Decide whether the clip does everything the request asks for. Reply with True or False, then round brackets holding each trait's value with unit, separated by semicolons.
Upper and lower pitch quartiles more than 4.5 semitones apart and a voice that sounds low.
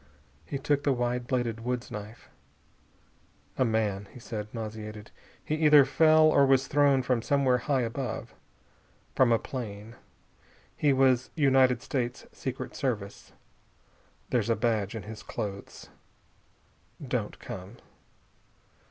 False (3.4 semitones; 125 Hz)